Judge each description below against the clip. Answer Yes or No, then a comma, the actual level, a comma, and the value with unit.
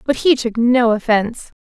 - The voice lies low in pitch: No, high, 235 Hz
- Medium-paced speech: Yes, average, 185 wpm